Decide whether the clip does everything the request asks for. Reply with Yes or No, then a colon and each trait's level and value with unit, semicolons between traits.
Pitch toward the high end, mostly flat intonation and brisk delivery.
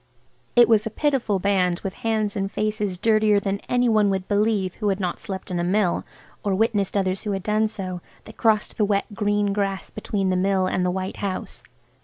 Yes: high, 200 Hz; narrow, 2.1 semitones; fast, 210 wpm